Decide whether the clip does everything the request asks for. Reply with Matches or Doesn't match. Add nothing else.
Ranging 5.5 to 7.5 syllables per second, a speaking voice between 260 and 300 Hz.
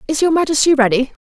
Matches